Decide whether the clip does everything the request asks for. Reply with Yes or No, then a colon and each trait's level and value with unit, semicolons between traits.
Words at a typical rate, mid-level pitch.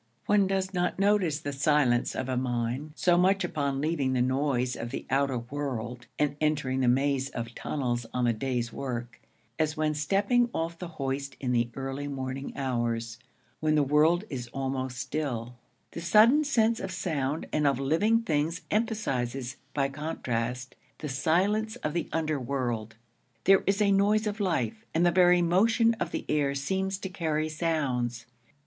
Yes: average, 165 wpm; medium, 145 Hz